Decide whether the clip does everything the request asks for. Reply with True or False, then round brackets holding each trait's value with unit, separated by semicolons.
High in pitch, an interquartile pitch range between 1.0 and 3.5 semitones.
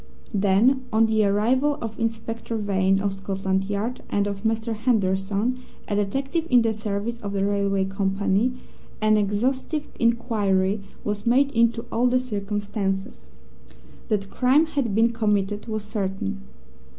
True (210 Hz; 2.9 semitones)